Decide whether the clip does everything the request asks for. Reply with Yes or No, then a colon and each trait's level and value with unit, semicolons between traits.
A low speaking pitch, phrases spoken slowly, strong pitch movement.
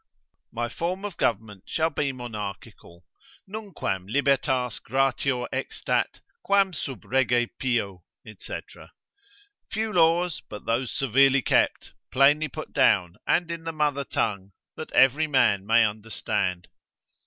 Yes: low, 130 Hz; slow, 120 wpm; wide, 6.3 semitones